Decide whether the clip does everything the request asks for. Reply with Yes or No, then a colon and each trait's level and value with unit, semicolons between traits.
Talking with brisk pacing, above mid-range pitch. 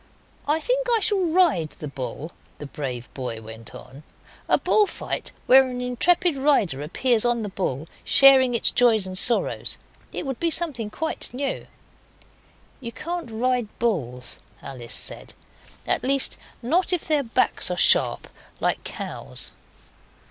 No: average, 150 wpm; high, 245 Hz